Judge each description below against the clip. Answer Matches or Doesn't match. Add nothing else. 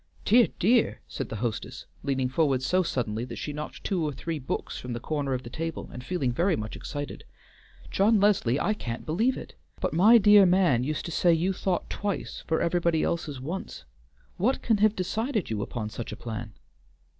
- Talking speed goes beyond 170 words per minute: Matches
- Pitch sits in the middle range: Matches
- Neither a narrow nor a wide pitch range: Doesn't match